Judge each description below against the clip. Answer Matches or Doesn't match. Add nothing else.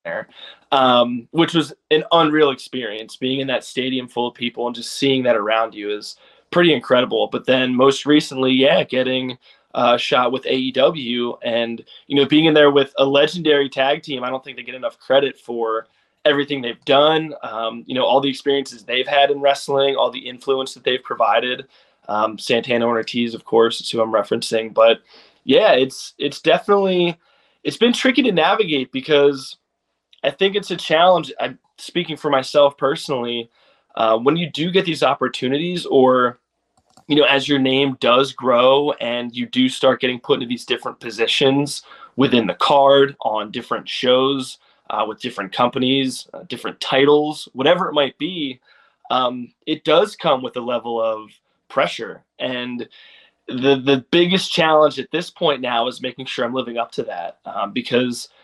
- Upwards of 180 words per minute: Doesn't match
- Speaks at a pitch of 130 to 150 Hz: Matches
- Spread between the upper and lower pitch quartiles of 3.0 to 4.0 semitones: Matches